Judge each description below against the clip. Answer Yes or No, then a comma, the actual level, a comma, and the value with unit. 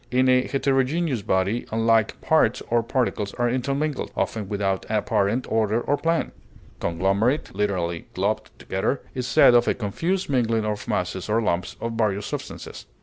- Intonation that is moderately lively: Yes, average, 4.1 semitones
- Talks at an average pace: Yes, average, 150 wpm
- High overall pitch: No, low, 115 Hz